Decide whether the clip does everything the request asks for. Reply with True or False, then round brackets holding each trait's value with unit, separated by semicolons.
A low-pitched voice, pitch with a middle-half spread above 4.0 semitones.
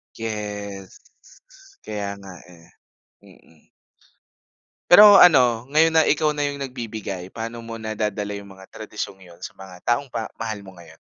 True (110 Hz; 4.4 semitones)